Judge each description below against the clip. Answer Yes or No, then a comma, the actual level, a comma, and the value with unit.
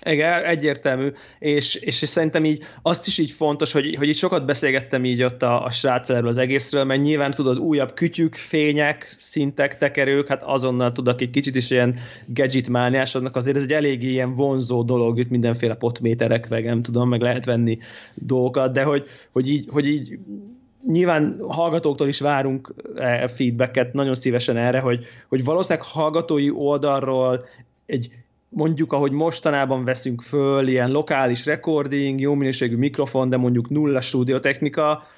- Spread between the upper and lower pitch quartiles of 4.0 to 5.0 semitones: No, average, 2.9 semitones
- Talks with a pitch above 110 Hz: Yes, low, 135 Hz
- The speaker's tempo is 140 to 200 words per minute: Yes, average, 150 wpm